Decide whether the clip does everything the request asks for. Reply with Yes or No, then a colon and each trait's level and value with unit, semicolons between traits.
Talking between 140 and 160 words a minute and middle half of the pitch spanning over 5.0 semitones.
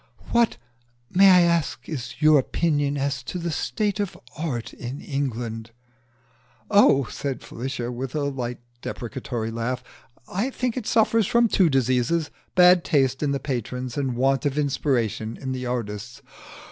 Yes: average, 150 wpm; wide, 5.4 semitones